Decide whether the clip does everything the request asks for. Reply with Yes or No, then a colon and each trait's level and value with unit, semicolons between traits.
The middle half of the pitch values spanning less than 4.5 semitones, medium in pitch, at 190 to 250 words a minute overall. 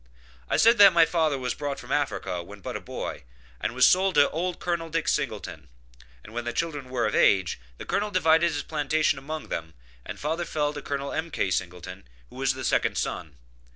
No: average, 5.1 semitones; medium, 145 Hz; fast, 205 wpm